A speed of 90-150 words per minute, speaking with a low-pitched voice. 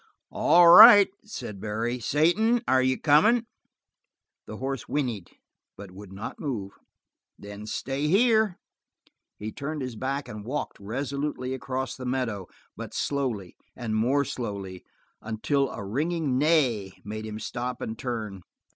Yes: slow, 135 wpm; low, 130 Hz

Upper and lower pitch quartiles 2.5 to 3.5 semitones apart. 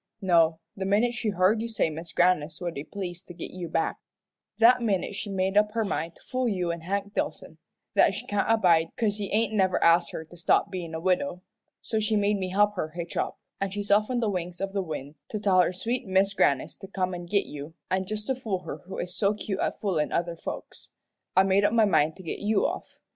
Yes: average, 3.2 semitones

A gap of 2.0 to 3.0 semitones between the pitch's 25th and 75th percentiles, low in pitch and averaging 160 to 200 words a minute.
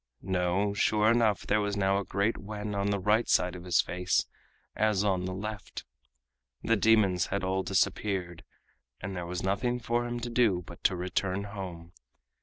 Yes: narrow, 2.6 semitones; low, 100 Hz; average, 180 wpm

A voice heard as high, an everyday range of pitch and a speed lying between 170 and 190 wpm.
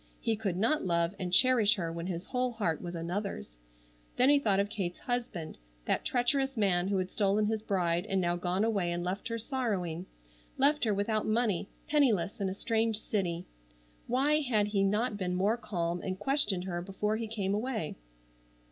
Yes: high, 200 Hz; average, 4.3 semitones; average, 185 wpm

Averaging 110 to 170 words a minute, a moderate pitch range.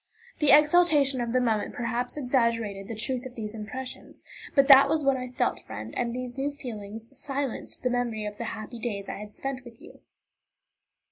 No: average, 190 wpm; average, 3.5 semitones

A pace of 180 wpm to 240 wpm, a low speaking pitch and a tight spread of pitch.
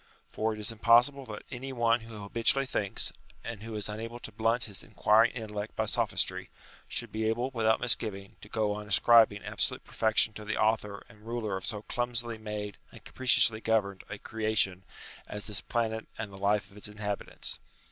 Yes: average, 185 wpm; low, 110 Hz; narrow, 1.9 semitones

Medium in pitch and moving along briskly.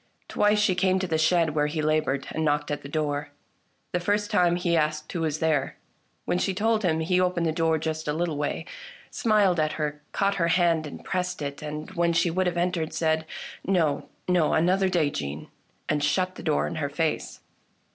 Yes: medium, 165 Hz; fast, 215 wpm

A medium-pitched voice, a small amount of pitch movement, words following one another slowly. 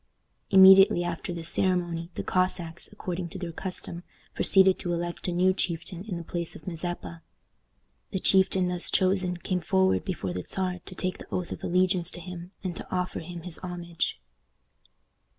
No: medium, 180 Hz; narrow, 1.5 semitones; average, 170 wpm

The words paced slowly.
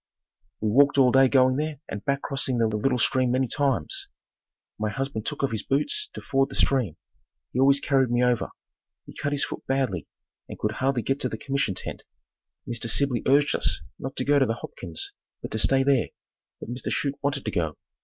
No: fast, 205 wpm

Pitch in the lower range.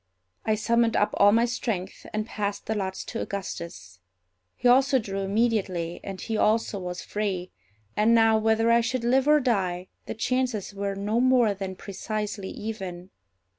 No: high, 215 Hz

